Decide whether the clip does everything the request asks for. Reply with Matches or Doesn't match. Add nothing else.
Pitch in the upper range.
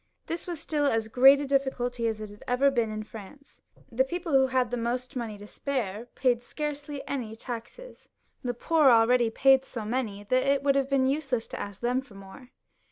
Matches